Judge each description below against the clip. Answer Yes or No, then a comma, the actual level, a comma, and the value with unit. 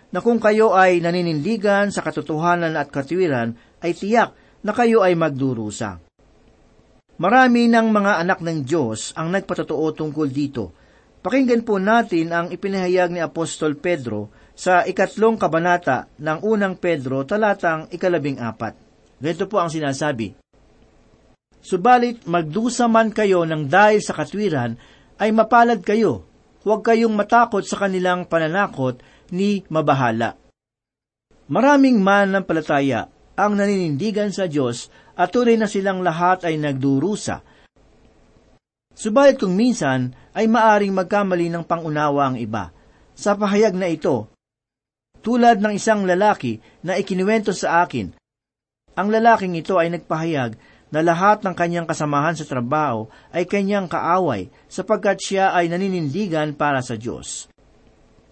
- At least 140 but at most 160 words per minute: No, average, 130 wpm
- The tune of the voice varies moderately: No, wide, 5.8 semitones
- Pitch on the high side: No, medium, 175 Hz